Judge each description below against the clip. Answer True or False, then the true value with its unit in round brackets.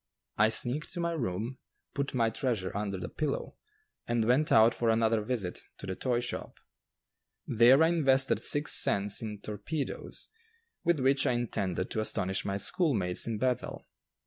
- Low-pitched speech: True (120 Hz)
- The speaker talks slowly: False (160 wpm)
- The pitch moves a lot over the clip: False (4.4 semitones)